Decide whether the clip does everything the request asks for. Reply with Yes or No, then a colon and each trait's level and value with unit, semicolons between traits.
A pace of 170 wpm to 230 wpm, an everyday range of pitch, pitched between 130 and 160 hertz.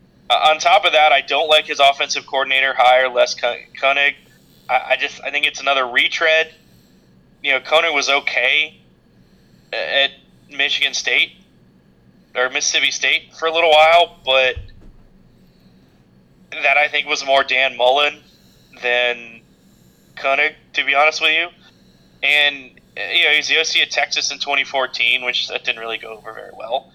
No: average, 155 wpm; average, 3.2 semitones; low, 135 Hz